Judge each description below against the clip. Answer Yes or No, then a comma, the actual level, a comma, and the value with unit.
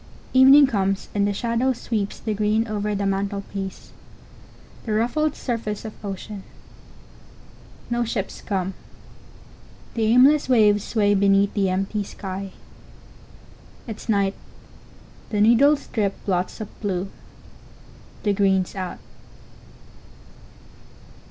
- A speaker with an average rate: No, slow, 105 wpm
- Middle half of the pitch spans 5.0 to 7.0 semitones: No, average, 2.7 semitones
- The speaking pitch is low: No, high, 205 Hz